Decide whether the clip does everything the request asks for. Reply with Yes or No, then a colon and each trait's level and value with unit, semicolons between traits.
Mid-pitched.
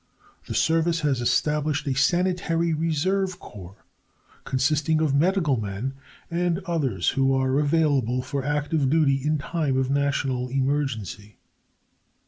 Yes: medium, 145 Hz